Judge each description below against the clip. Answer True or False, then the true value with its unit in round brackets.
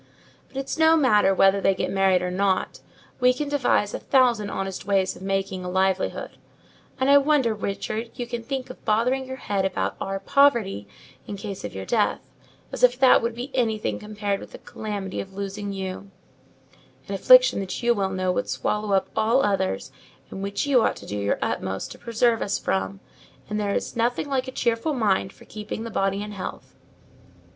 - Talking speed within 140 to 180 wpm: False (195 wpm)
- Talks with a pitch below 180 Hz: False (210 Hz)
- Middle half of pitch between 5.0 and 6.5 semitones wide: False (4.2 semitones)